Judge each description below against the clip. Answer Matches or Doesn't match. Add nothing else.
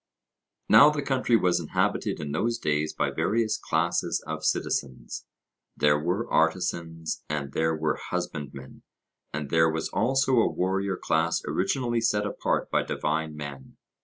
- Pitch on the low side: Matches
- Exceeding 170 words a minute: Doesn't match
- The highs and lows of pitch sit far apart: Matches